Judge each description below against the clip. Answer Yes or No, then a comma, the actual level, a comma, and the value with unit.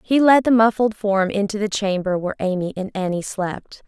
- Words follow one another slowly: No, average, 200 wpm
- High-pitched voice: Yes, high, 205 Hz